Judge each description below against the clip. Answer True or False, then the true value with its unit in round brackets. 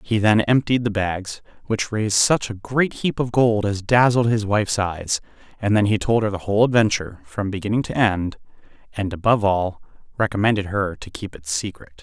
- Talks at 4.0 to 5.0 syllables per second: False (5.4 syllables/s)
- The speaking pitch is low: True (105 Hz)